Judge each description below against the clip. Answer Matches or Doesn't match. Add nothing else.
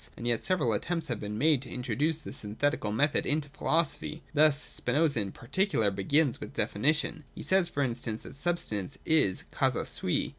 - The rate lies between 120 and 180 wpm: Doesn't match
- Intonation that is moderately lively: Doesn't match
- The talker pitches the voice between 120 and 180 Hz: Matches